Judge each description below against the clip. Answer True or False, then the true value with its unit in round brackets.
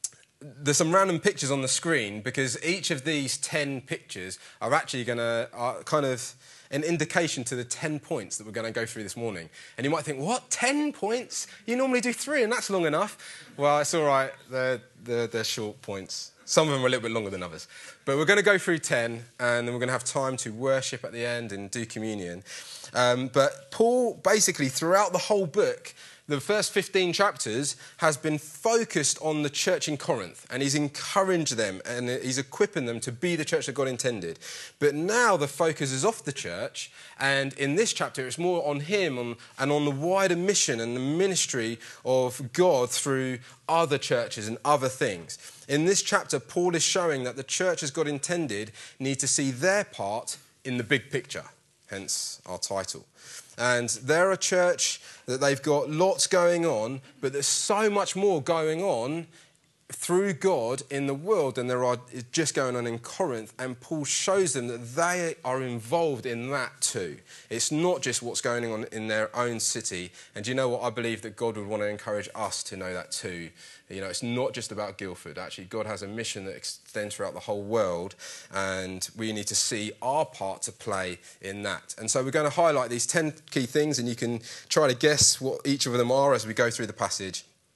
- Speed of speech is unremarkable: False (210 wpm)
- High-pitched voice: False (135 Hz)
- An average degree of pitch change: False (5.7 semitones)